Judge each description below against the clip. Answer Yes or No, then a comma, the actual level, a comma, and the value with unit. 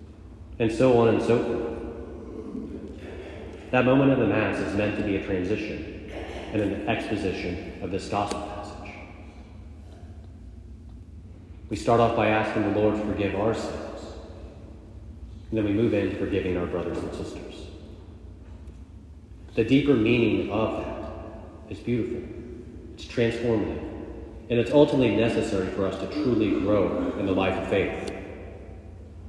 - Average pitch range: Yes, average, 4.2 semitones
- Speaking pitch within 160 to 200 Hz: No, low, 100 Hz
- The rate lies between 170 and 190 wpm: No, average, 140 wpm